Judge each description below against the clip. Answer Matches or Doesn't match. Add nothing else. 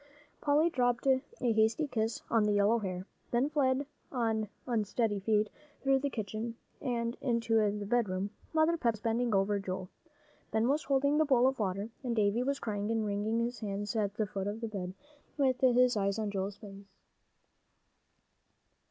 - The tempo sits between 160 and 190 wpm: Matches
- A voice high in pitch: Matches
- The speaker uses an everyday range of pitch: Matches